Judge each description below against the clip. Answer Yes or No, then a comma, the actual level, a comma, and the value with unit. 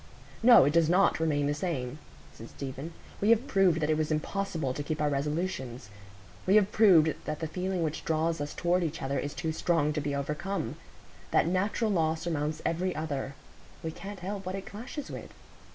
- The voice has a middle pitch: Yes, medium, 160 Hz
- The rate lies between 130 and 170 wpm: No, average, 195 wpm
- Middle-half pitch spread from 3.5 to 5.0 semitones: Yes, average, 4.1 semitones